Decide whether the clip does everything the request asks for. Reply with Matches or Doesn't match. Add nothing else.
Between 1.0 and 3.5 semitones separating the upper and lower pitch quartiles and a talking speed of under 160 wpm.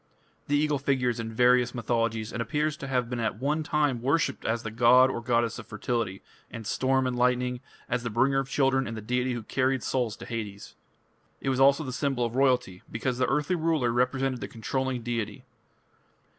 Doesn't match